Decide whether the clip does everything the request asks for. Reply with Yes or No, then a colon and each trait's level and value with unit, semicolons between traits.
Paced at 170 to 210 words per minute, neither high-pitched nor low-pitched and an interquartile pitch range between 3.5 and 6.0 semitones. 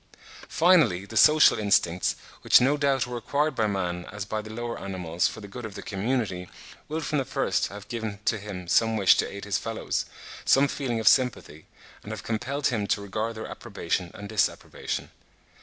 No: average, 190 wpm; low, 110 Hz; average, 3.8 semitones